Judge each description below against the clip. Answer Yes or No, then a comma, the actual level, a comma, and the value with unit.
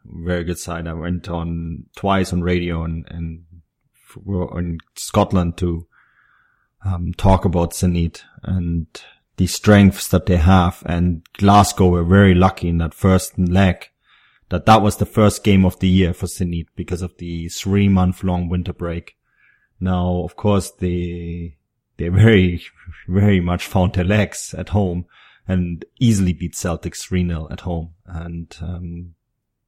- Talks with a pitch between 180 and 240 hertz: No, very low, 90 Hz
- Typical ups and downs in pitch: No, narrow, 1.9 semitones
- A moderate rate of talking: Yes, average, 150 wpm